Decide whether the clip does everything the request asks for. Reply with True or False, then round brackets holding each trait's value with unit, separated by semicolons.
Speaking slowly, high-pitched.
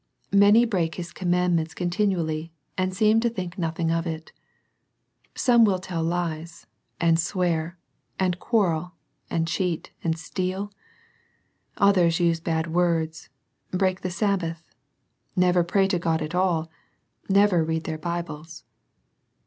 False (130 wpm; 175 Hz)